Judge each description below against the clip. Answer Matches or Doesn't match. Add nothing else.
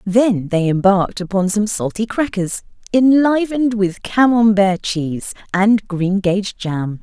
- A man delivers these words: Doesn't match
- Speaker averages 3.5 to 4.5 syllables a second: Matches